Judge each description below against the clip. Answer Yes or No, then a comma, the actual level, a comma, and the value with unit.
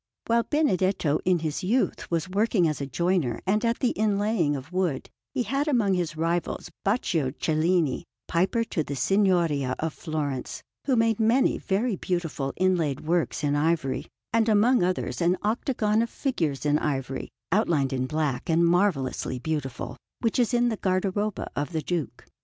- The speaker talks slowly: No, average, 165 wpm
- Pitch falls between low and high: Yes, medium, 175 Hz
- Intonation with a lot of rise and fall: Yes, wide, 5.9 semitones